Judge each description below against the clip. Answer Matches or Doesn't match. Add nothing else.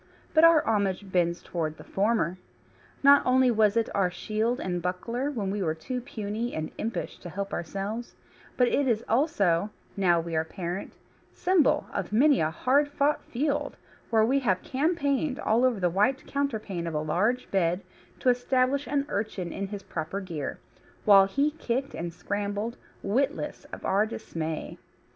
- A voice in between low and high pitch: Doesn't match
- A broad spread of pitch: Matches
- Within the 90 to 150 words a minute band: Doesn't match